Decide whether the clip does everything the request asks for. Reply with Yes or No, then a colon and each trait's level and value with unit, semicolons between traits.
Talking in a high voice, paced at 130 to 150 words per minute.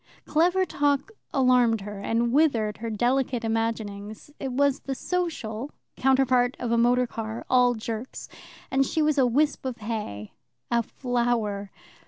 Yes: high, 245 Hz; average, 140 wpm